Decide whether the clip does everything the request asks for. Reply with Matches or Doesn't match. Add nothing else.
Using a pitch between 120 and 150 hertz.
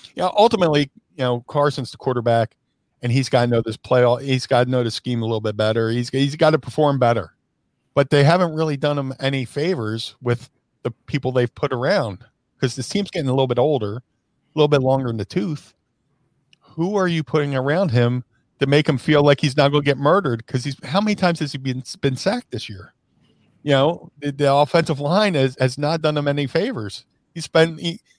Matches